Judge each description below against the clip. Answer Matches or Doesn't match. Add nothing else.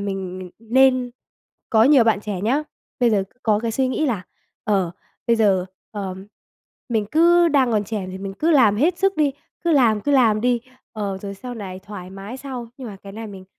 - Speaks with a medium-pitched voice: Doesn't match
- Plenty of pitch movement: Doesn't match